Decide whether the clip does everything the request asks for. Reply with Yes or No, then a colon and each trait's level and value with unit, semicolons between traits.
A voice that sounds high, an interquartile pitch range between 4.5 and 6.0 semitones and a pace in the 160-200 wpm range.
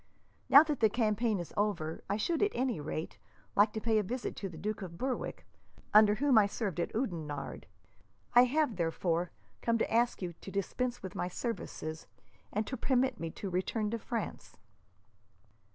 Yes: high, 215 Hz; average, 5.3 semitones; average, 180 wpm